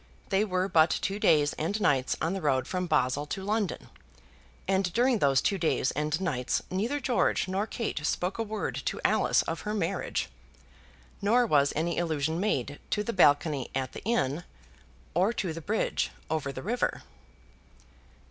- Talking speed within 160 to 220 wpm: Yes, average, 165 wpm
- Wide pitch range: Yes, wide, 5.9 semitones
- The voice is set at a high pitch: No, medium, 175 Hz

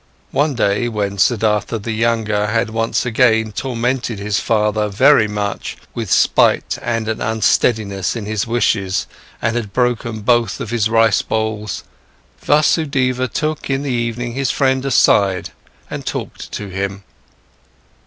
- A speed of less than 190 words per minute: Yes, average, 140 wpm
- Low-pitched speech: Yes, low, 110 Hz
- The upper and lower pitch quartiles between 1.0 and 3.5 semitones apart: Yes, average, 2.7 semitones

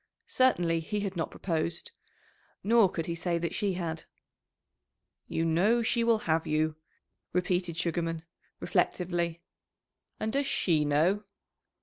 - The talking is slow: Yes, slow, 125 wpm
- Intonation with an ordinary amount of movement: Yes, average, 3.6 semitones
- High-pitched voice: No, medium, 170 Hz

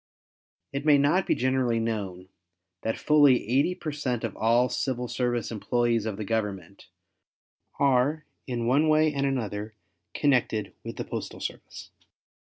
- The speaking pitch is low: Yes, low, 125 Hz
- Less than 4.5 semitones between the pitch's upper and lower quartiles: Yes, average, 3.9 semitones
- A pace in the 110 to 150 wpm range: Yes, average, 145 wpm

